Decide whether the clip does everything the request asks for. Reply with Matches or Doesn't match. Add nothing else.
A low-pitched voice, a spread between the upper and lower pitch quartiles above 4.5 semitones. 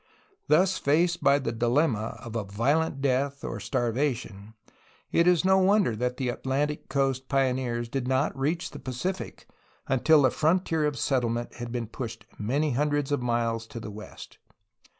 Doesn't match